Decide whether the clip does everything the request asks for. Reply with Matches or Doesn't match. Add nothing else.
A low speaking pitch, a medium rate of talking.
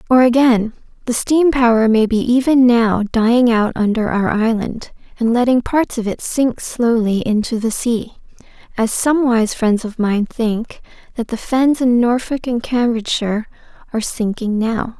Doesn't match